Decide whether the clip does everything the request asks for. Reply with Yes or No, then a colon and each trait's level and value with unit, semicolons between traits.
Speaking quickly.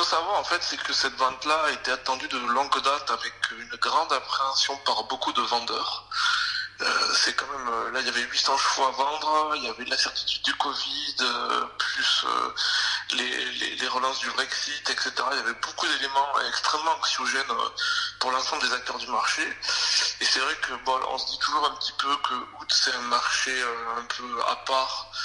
No: average, 195 wpm